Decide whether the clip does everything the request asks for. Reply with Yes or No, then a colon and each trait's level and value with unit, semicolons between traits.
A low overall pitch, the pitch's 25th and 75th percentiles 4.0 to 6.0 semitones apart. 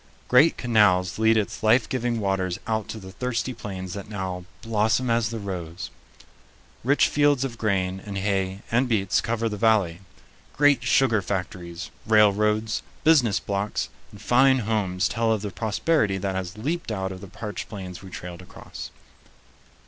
No: low, 105 Hz; average, 3.3 semitones